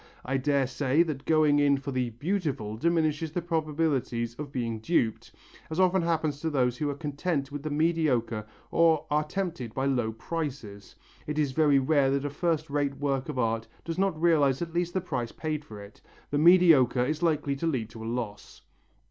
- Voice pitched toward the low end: No, medium, 145 Hz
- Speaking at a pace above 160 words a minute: Yes, average, 195 wpm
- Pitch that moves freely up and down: No, average, 4.0 semitones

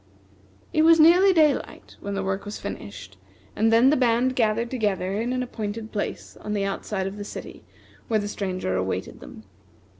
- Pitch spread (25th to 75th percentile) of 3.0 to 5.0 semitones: Yes, average, 4.3 semitones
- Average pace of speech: Yes, average, 180 wpm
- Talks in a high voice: Yes, high, 210 Hz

